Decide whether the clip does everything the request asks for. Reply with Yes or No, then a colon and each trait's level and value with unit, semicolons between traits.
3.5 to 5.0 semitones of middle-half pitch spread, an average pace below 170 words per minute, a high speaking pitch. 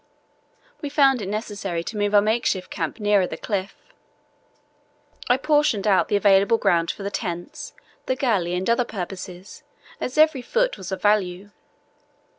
Yes: average, 4.3 semitones; average, 155 wpm; high, 205 Hz